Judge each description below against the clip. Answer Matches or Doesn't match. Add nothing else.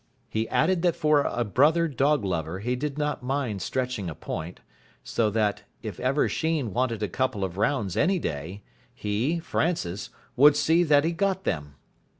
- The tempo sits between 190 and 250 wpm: Doesn't match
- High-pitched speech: Doesn't match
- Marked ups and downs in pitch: Matches